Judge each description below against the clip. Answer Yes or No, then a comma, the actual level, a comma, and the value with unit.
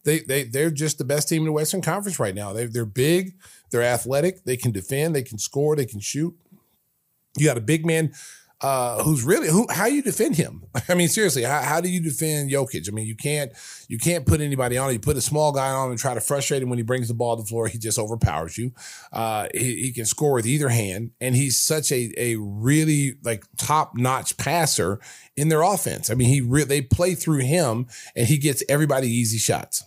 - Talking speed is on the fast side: Yes, fast, 235 wpm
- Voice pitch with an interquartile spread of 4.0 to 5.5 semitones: Yes, average, 4.4 semitones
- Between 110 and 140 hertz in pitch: Yes, low, 135 Hz